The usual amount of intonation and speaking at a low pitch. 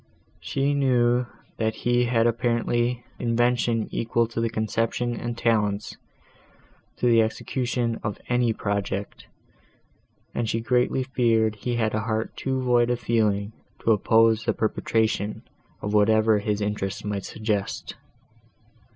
No: narrow, 2.0 semitones; low, 115 Hz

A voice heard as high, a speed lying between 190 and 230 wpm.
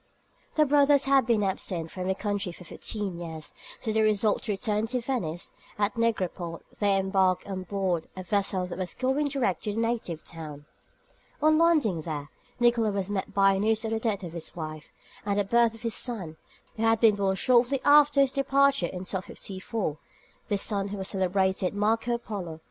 Yes: high, 205 Hz; average, 195 wpm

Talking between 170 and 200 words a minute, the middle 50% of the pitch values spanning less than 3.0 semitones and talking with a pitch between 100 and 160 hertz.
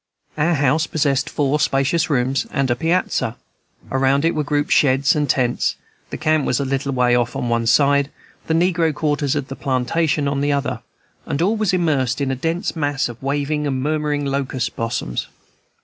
Yes: average, 185 wpm; narrow, 2.6 semitones; medium, 140 Hz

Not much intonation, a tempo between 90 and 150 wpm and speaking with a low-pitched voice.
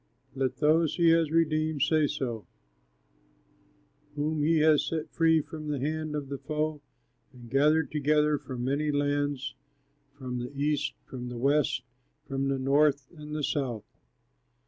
No: narrow, 2.2 semitones; average, 145 wpm; medium, 145 Hz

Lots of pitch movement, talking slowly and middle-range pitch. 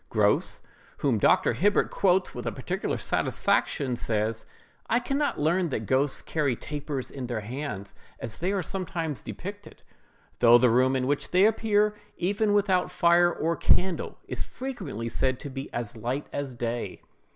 No: wide, 7.3 semitones; average, 165 wpm; medium, 145 Hz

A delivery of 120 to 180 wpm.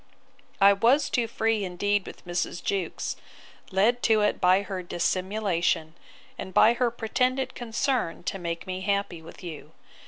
Yes: average, 150 wpm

